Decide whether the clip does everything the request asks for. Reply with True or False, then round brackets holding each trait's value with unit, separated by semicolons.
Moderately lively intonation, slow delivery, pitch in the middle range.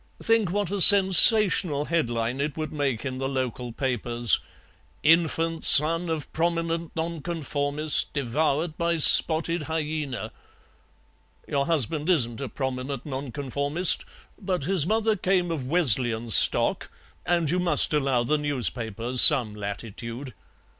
True (4.6 semitones; 120 wpm; 150 Hz)